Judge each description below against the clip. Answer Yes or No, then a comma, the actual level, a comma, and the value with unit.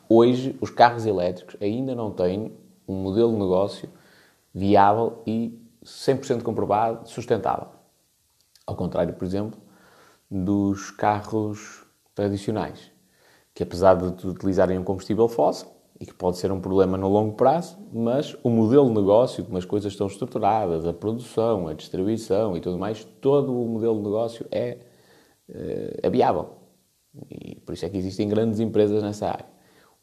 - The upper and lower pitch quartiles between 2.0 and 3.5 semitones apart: Yes, average, 3.1 semitones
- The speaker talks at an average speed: Yes, average, 150 wpm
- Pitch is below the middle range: Yes, low, 105 Hz